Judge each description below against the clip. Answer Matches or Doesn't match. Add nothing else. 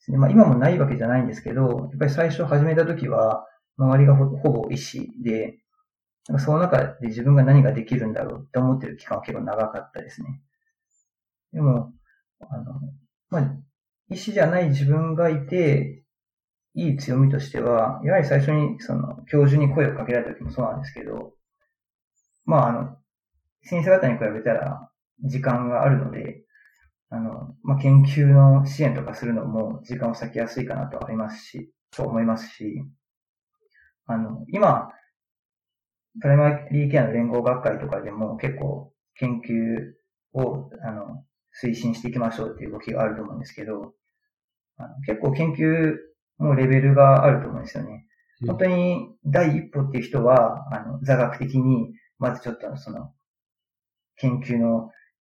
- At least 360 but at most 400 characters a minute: Doesn't match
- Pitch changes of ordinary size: Matches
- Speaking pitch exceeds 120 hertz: Matches